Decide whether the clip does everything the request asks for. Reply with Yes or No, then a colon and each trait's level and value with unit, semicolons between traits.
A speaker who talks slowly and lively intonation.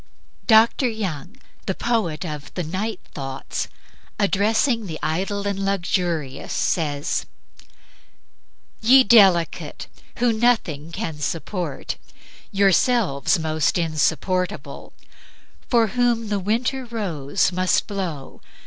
Yes: slow, 100 wpm; wide, 5.7 semitones